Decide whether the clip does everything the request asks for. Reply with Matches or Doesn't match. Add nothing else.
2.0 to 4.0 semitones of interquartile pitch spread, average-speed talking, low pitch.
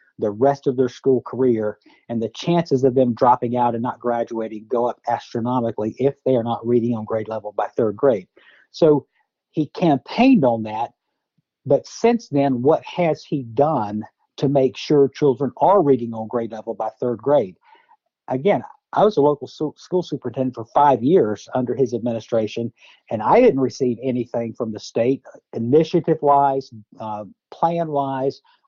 Matches